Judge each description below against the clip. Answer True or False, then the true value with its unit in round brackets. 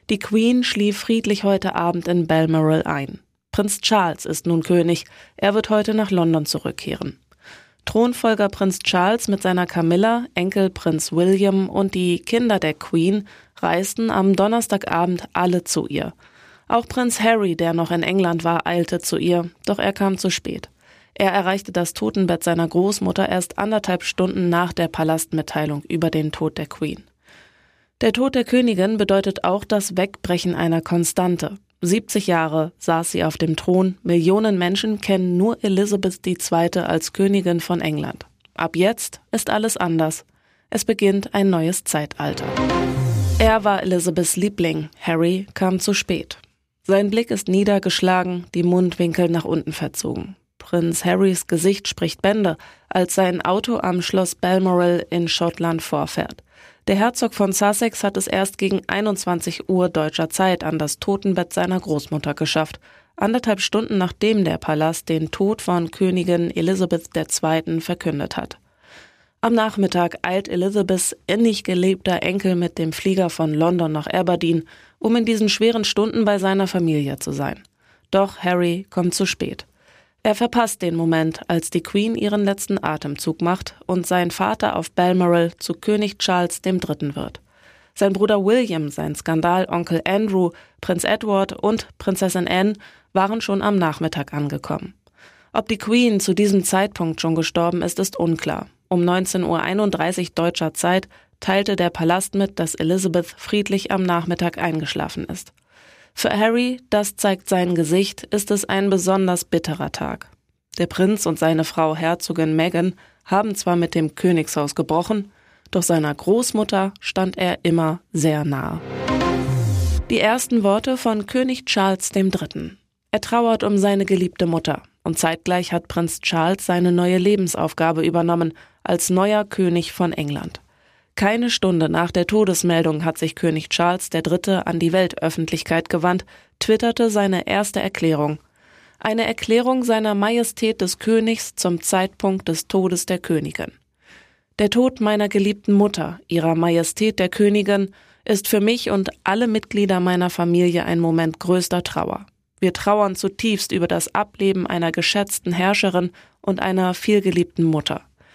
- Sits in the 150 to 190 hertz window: True (185 Hz)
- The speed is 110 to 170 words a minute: True (145 wpm)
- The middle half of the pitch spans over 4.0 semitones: False (3.1 semitones)